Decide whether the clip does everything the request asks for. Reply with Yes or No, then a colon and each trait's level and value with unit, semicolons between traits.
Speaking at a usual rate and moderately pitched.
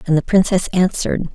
Yes: average, 180 wpm; medium, 180 Hz